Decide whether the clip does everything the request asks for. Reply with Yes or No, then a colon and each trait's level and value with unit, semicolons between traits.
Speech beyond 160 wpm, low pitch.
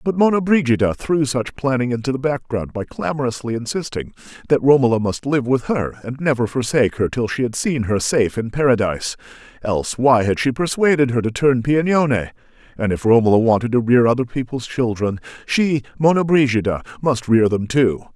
Yes: average, 175 wpm; low, 125 Hz